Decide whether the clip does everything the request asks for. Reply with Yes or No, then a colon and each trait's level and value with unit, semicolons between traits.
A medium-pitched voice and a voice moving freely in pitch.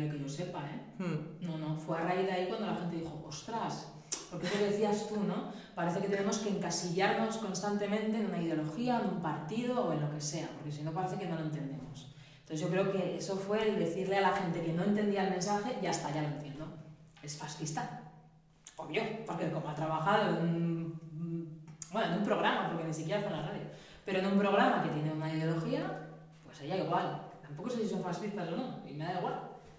No: medium, 175 Hz; average, 4.2 semitones